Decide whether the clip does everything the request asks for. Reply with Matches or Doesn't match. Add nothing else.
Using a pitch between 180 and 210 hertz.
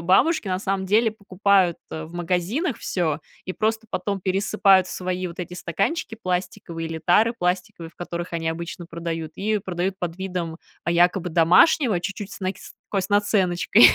Matches